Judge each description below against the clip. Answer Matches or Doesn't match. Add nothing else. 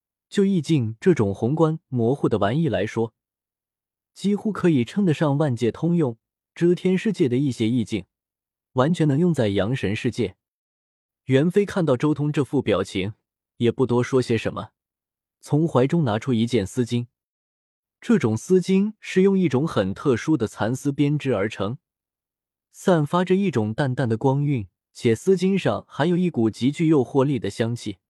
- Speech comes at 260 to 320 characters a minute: Doesn't match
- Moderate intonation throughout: Doesn't match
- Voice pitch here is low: Matches